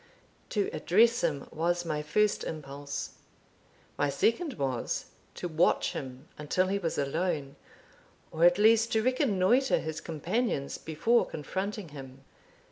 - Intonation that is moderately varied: No, wide, 6.4 semitones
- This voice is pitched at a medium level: Yes, medium, 170 Hz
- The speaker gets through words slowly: Yes, slow, 125 wpm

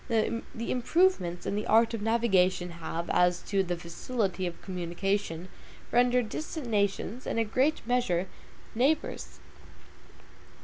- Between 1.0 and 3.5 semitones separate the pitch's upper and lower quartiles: No, average, 5.2 semitones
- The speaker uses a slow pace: Yes, slow, 125 wpm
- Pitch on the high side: Yes, high, 210 Hz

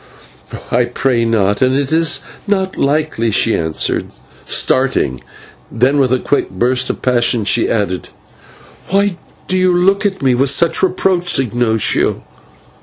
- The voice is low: Yes, low, 130 Hz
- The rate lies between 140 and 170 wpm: Yes, average, 145 wpm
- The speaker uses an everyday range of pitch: No, wide, 7.1 semitones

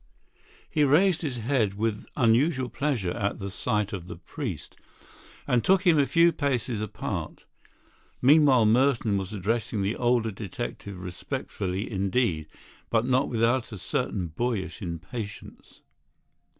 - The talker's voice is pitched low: Yes, low, 115 Hz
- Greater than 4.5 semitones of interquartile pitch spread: Yes, average, 4.9 semitones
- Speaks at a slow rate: Yes, slow, 130 wpm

